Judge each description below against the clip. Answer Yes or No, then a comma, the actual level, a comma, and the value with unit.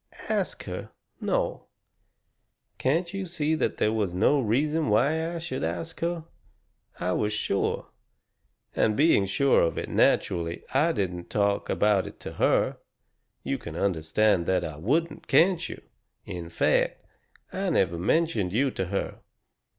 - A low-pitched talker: Yes, low, 110 Hz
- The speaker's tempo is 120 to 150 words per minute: Yes, average, 145 wpm